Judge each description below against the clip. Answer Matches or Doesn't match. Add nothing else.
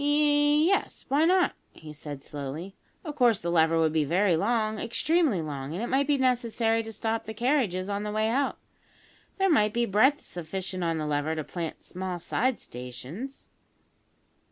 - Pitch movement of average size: Doesn't match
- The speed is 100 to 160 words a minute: Doesn't match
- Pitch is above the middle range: Matches